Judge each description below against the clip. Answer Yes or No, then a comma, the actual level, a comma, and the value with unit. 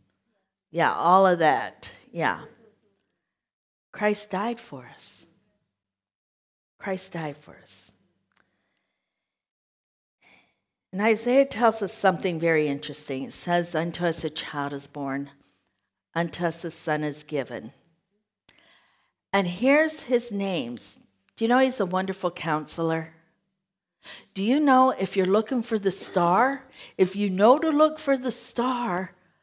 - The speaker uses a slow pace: Yes, slow, 125 wpm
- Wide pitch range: Yes, wide, 5.9 semitones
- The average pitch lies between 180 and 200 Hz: Yes, medium, 185 Hz